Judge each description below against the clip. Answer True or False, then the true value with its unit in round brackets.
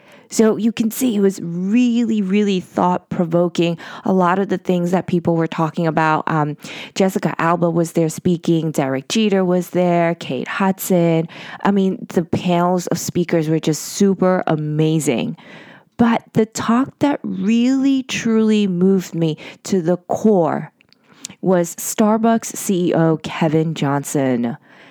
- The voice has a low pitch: False (180 Hz)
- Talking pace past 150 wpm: False (140 wpm)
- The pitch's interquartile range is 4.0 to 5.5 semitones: True (4.3 semitones)